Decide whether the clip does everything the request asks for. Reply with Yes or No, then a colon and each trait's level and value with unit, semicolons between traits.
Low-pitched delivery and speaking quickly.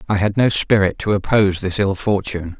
Yes: low, 100 Hz; fast, 210 wpm